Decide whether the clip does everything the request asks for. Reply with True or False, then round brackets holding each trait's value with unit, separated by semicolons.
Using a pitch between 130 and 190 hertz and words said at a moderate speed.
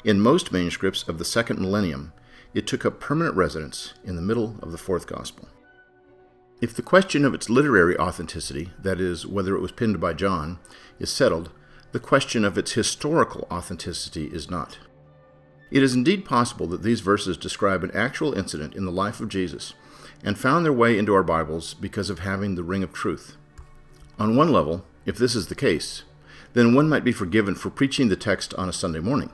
False (95 Hz; 195 wpm)